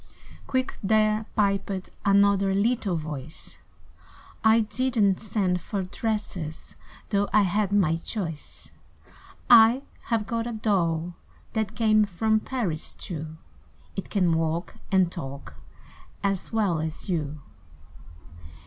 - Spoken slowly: Yes, slow, 115 wpm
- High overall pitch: Yes, high, 200 Hz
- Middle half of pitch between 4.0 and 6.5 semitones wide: Yes, average, 4.3 semitones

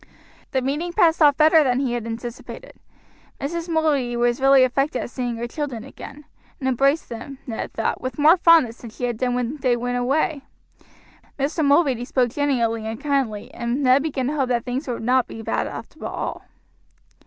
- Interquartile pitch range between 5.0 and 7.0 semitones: No, average, 3.3 semitones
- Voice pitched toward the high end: Yes, very high, 260 Hz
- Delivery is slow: No, average, 190 wpm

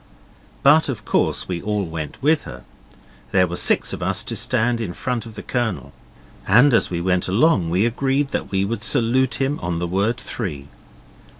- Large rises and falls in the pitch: Yes, wide, 5.8 semitones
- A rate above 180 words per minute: Yes, average, 195 wpm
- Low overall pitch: Yes, low, 110 Hz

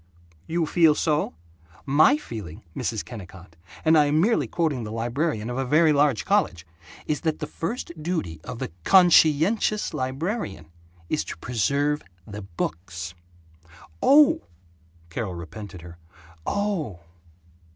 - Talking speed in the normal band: No, slow, 130 wpm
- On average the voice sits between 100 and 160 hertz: Yes, medium, 140 Hz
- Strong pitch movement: Yes, wide, 8.8 semitones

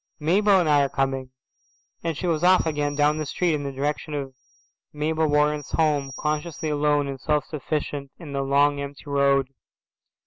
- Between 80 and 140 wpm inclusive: No, average, 175 wpm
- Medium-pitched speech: Yes, medium, 150 Hz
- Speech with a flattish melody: Yes, narrow, 1.8 semitones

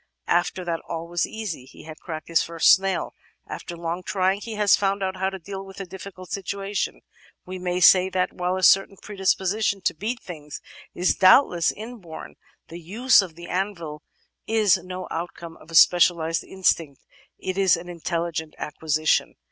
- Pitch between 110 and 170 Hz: No, medium, 185 Hz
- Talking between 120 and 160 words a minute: No, average, 175 wpm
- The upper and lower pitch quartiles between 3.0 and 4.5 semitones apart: No, narrow, 2.5 semitones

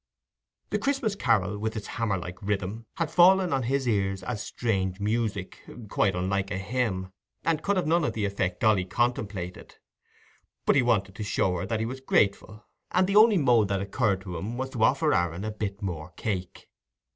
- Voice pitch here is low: Yes, low, 105 Hz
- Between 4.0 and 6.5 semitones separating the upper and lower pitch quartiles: Yes, average, 4.9 semitones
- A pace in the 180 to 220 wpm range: Yes, average, 190 wpm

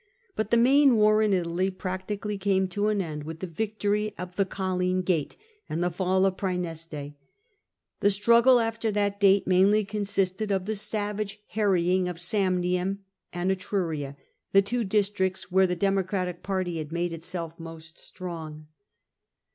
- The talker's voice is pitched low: No, high, 190 Hz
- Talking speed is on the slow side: No, average, 155 wpm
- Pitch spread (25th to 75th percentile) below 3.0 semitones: Yes, narrow, 2.6 semitones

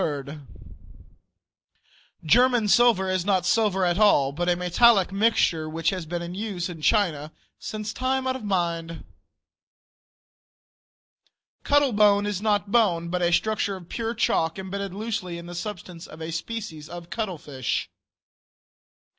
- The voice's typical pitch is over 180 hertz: Yes, high, 190 Hz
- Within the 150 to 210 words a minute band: No, slow, 135 wpm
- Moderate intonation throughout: Yes, average, 4.0 semitones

